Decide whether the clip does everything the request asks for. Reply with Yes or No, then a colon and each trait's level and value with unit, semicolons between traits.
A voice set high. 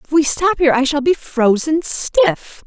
Yes: very high, 280 Hz